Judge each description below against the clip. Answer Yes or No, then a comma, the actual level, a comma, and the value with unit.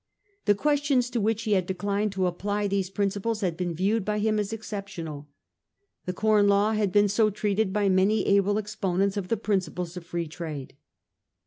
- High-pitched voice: Yes, high, 200 Hz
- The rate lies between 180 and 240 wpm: Yes, average, 185 wpm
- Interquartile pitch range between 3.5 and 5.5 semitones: No, narrow, 2.4 semitones